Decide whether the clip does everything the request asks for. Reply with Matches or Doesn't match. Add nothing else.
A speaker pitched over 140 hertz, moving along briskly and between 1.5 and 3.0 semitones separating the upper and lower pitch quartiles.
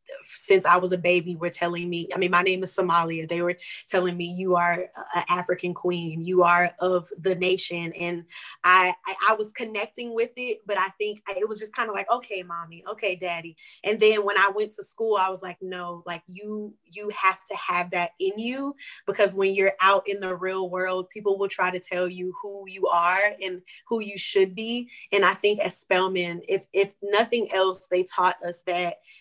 Matches